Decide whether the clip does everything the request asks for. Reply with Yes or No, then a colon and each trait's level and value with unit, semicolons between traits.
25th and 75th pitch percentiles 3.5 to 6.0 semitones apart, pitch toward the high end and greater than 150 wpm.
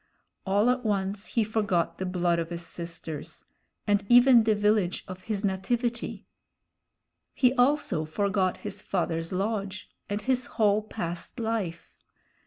No: average, 3.8 semitones; high, 200 Hz; slow, 135 wpm